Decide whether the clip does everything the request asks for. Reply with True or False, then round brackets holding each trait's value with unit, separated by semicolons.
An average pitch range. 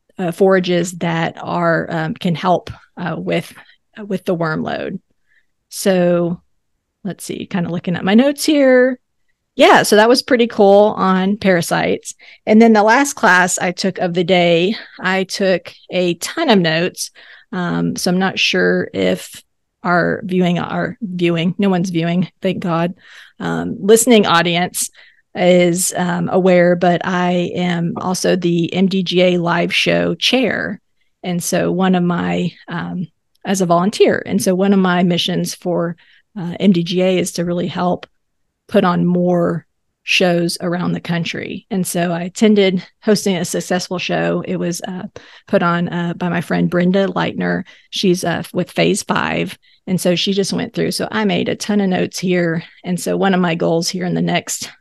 False (2.0 semitones)